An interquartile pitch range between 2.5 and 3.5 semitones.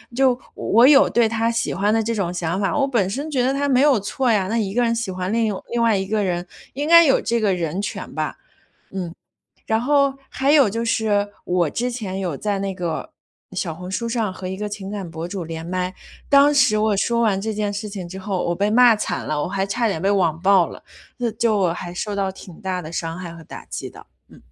No: average, 4.1 semitones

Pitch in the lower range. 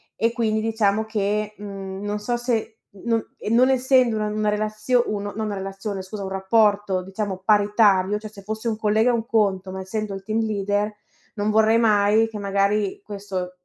No: high, 210 Hz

